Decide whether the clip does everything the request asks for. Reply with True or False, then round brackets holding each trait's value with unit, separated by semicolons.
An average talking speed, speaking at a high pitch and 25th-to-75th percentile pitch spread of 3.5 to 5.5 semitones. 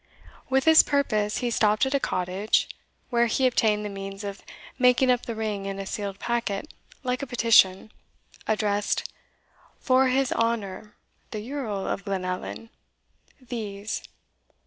True (145 wpm; 220 Hz; 3.9 semitones)